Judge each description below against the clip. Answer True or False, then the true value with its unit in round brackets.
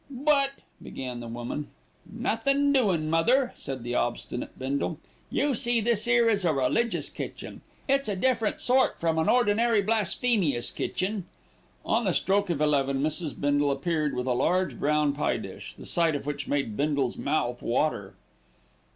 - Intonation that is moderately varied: False (8.5 semitones)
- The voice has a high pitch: False (165 Hz)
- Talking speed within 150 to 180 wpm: True (160 wpm)